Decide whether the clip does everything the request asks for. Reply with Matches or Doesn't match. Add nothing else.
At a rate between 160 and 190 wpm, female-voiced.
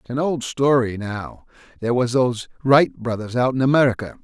Doesn't match